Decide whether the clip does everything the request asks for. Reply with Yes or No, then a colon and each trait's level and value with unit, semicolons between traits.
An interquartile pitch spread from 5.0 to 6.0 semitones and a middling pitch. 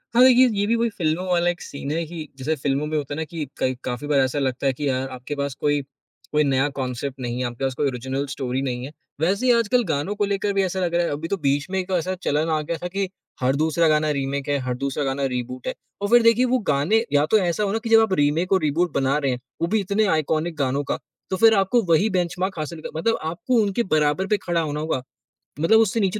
Yes: wide, 5.4 semitones; medium, 155 Hz